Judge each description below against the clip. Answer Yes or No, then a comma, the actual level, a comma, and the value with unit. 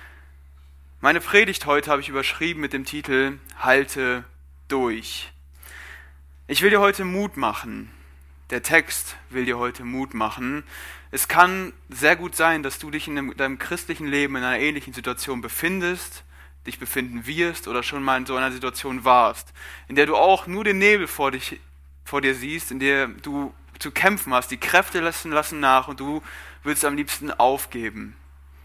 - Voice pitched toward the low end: Yes, low, 130 Hz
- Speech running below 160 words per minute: No, average, 170 wpm